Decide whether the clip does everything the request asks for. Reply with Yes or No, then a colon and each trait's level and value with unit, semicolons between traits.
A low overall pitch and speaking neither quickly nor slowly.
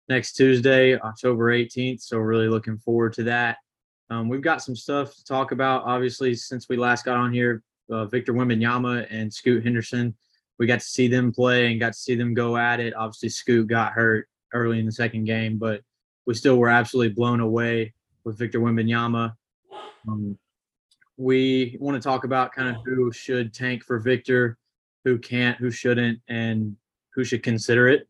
Yes: low, 120 Hz; average, 185 wpm